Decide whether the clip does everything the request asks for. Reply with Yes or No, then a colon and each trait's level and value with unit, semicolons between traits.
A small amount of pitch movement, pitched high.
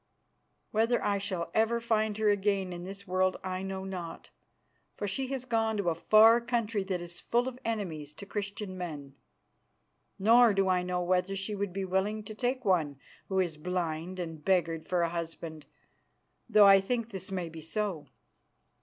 No: average, 3.4 semitones; high, 195 Hz